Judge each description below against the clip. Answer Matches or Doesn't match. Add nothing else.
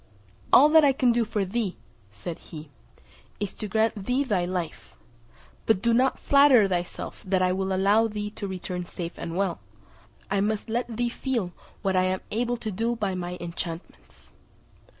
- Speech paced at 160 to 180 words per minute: Matches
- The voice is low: Doesn't match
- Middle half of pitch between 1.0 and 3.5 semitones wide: Doesn't match